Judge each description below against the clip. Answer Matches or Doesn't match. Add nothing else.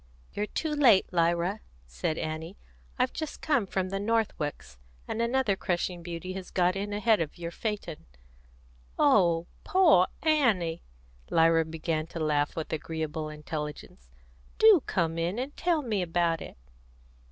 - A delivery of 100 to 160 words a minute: Matches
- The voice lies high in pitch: Doesn't match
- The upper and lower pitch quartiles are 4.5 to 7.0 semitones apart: Matches